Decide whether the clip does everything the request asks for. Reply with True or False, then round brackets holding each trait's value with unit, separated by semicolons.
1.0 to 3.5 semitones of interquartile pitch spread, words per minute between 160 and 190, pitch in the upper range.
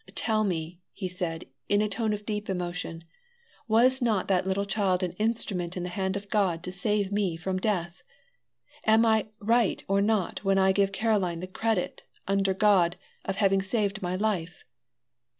True (2.7 semitones; 175 wpm; 195 Hz)